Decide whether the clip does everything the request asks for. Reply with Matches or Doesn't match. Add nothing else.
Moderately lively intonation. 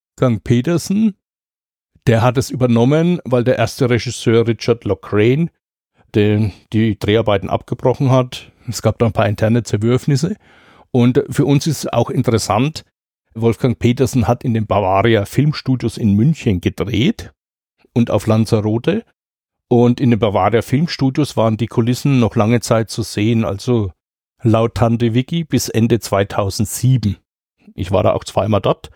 Matches